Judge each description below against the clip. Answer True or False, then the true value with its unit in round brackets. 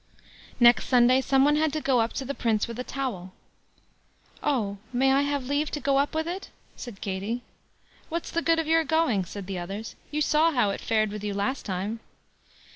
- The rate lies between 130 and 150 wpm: False (205 wpm)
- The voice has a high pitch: True (255 Hz)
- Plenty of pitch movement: True (5.8 semitones)